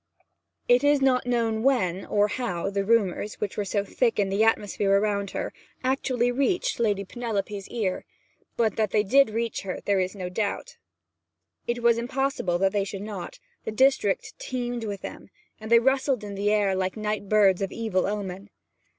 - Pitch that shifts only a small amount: No, average, 3.4 semitones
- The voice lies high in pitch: Yes, high, 210 Hz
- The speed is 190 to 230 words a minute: No, average, 180 wpm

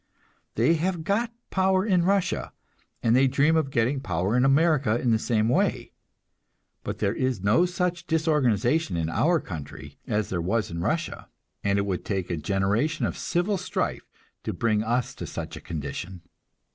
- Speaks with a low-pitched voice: Yes, low, 120 Hz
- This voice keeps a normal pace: Yes, average, 170 wpm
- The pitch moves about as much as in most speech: No, wide, 8.5 semitones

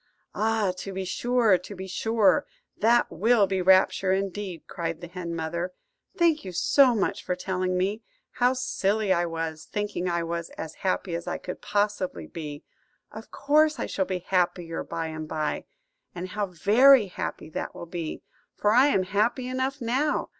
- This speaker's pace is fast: No, average, 175 wpm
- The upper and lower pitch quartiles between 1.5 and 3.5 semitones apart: No, average, 4.3 semitones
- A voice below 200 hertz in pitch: Yes, high, 190 Hz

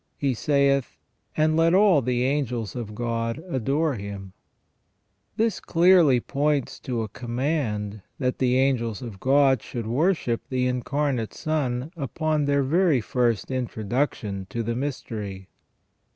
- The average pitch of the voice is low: Yes, low, 130 Hz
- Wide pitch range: No, average, 4.0 semitones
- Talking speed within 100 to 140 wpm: Yes, slow, 135 wpm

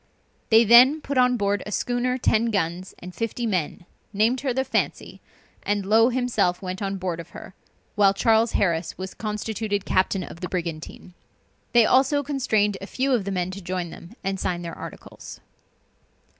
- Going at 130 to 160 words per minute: No, average, 175 wpm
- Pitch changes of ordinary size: Yes, average, 4.4 semitones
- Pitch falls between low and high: No, high, 205 Hz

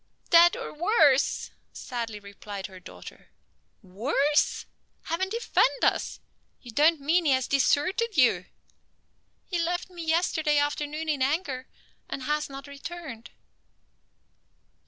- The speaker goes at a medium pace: No, slow, 115 wpm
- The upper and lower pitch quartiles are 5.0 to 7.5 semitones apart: No, average, 4.5 semitones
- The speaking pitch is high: Yes, very high, 295 Hz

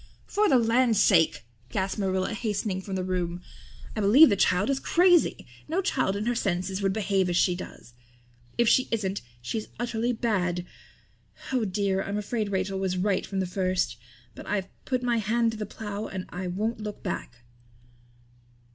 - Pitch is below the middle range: No, high, 200 Hz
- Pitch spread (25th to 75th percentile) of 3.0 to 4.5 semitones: Yes, average, 3.4 semitones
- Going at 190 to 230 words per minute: No, average, 175 wpm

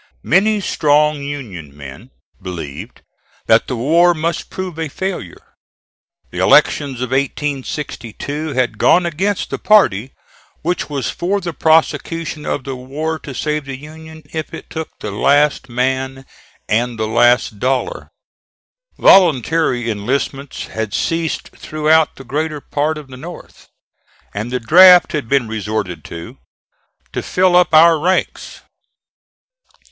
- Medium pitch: Yes, medium, 145 Hz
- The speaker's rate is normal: No, slow, 130 wpm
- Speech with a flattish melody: No, average, 4.7 semitones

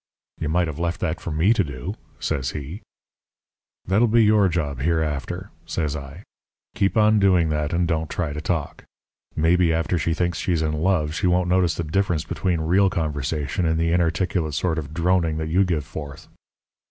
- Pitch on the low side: Yes, very low, 80 Hz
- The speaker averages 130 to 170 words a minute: No, average, 185 wpm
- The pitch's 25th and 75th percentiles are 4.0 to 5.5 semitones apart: No, average, 2.8 semitones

